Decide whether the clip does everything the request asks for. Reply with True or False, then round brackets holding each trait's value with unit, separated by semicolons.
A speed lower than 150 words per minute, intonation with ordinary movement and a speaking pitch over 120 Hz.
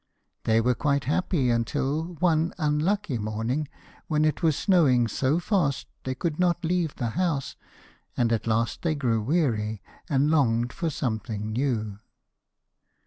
False (140 wpm; 5.7 semitones; 140 Hz)